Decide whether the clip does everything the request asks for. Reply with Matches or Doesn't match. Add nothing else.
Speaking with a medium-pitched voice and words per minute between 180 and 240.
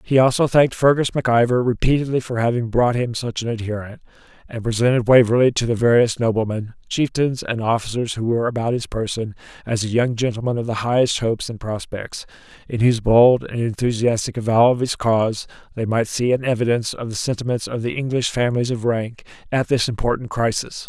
Doesn't match